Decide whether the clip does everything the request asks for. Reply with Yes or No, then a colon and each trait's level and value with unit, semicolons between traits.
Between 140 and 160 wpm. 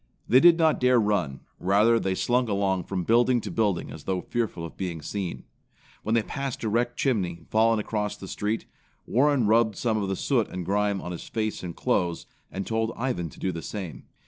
No: fast, 205 wpm